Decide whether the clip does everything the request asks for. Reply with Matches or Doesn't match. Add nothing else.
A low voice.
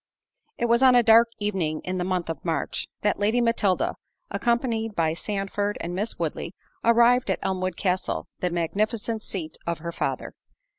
Doesn't match